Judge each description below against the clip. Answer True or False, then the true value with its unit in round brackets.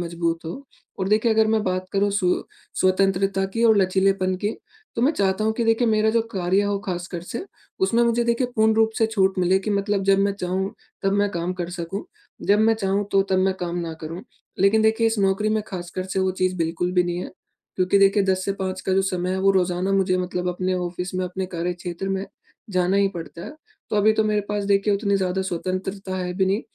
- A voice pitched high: True (195 Hz)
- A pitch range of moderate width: False (2.0 semitones)